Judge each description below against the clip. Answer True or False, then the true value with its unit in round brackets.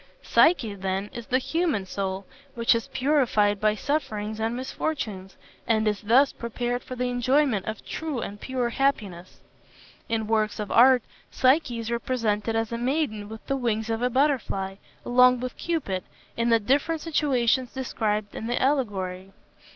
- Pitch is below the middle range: False (235 Hz)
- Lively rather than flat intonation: False (3.7 semitones)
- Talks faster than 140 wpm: True (160 wpm)